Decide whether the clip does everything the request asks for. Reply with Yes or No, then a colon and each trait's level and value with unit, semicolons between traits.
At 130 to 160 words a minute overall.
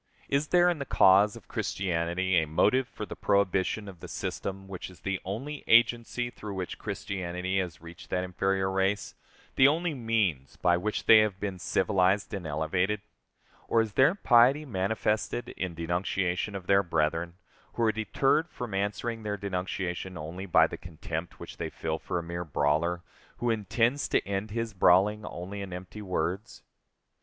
No: average, 170 wpm